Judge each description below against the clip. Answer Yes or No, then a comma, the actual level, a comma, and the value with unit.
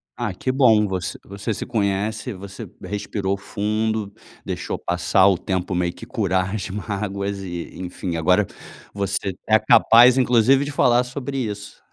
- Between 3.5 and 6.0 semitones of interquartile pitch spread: No, average, 3.0 semitones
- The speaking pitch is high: No, low, 100 Hz